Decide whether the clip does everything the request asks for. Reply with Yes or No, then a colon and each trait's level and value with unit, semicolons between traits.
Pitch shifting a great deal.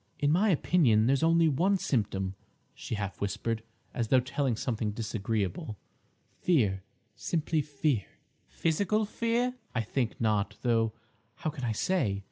Yes: wide, 6.9 semitones